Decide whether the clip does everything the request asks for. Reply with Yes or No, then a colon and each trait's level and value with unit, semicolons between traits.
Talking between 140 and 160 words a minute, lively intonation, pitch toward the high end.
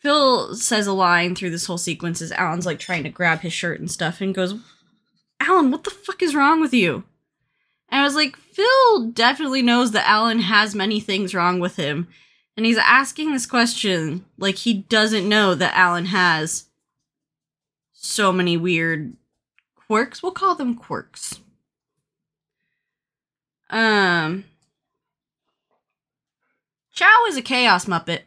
Yes: average, 145 wpm; wide, 6.1 semitones; high, 200 Hz